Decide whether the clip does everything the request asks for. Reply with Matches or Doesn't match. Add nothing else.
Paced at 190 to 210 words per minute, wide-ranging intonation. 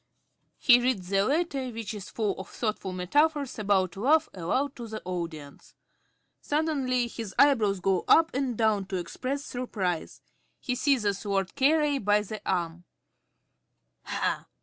Doesn't match